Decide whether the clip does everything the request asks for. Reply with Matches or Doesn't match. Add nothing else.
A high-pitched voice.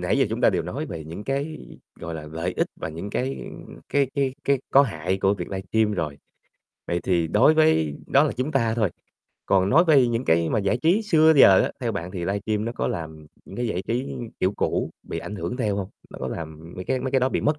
Doesn't match